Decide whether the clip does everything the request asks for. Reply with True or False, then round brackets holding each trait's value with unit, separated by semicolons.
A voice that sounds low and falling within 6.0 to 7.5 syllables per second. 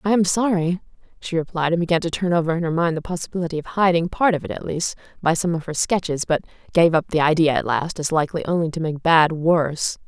False (165 Hz; 6.3 syllables/s)